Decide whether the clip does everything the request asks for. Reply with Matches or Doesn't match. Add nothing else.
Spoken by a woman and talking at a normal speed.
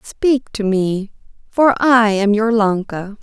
Matches